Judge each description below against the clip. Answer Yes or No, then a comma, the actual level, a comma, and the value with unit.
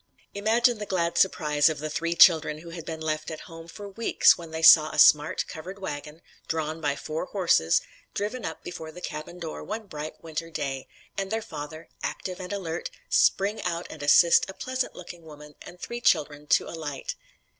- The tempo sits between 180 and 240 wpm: Yes, average, 190 wpm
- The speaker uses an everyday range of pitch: Yes, average, 3.6 semitones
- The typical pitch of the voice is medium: Yes, medium, 165 Hz